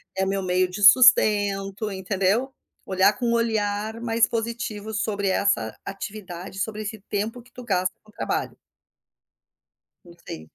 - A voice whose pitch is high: Yes, high, 205 Hz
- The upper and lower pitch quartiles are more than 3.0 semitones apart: No, average, 2.7 semitones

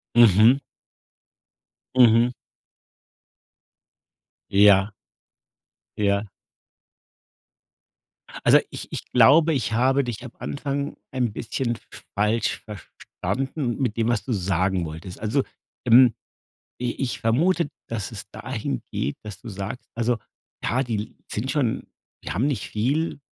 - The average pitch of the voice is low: Yes, low, 115 Hz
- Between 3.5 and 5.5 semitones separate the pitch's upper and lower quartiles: Yes, average, 4.0 semitones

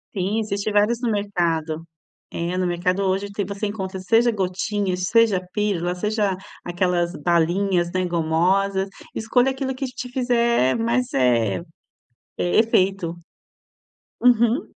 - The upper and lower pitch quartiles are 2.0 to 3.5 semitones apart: No, average, 4.0 semitones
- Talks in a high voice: Yes, high, 195 Hz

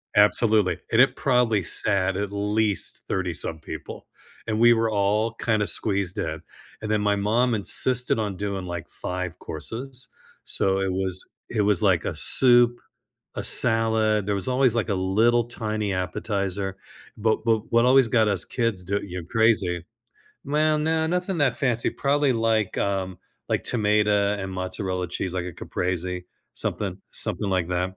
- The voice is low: Yes, low, 105 Hz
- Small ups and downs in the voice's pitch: No, average, 3.8 semitones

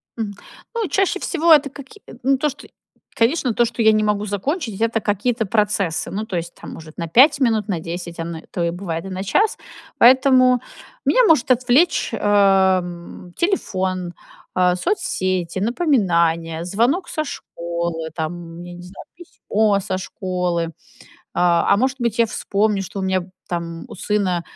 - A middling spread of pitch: No, wide, 6.1 semitones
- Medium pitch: No, high, 200 Hz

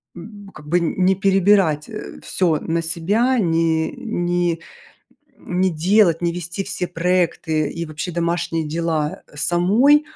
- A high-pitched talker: No, medium, 175 Hz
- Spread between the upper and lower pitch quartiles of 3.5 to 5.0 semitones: No, average, 2.9 semitones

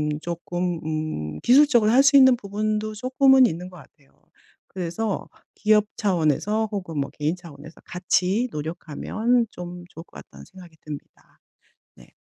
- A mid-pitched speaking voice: Yes, medium, 180 Hz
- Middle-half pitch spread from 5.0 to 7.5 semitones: Yes, wide, 5.4 semitones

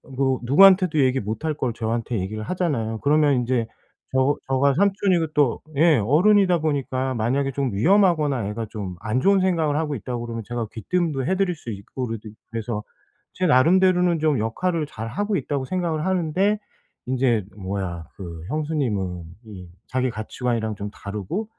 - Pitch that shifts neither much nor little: No, wide, 6.6 semitones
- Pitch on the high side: No, low, 130 Hz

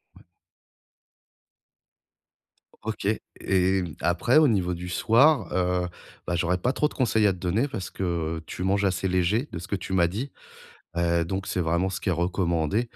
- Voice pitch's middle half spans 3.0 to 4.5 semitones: Yes, average, 3.5 semitones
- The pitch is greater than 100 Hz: No, very low, 95 Hz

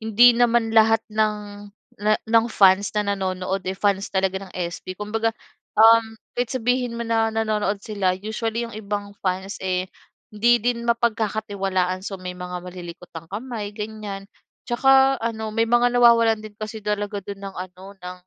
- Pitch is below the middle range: No, high, 210 Hz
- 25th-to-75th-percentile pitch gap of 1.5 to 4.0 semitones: Yes, average, 2.9 semitones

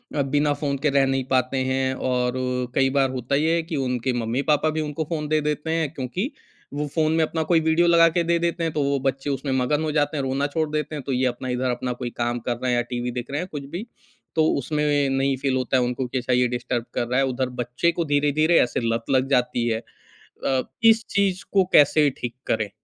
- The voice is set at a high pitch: No, medium, 140 Hz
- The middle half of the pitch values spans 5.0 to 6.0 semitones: No, average, 3.7 semitones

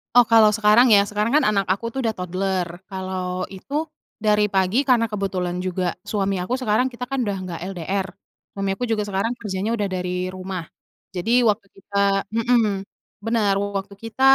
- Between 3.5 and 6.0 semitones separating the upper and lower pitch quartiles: No, average, 3.1 semitones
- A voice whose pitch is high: Yes, high, 200 Hz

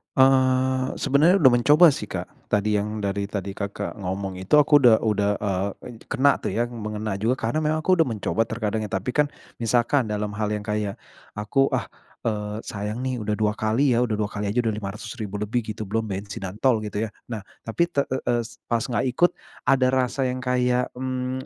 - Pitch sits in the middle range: No, low, 110 Hz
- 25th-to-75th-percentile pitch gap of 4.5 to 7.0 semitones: No, average, 3.7 semitones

